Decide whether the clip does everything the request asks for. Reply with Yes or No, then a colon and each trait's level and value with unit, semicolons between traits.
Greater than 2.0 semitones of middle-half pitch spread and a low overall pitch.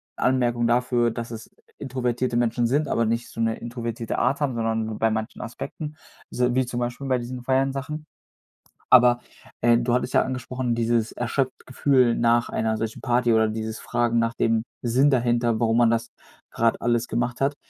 No: narrow, 1.7 semitones; low, 120 Hz